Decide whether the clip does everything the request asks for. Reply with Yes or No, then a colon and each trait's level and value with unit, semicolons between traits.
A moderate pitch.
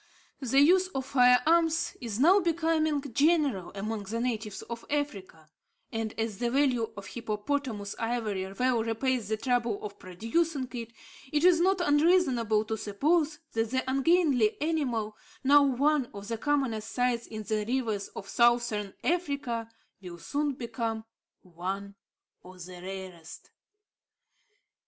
No: high, 235 Hz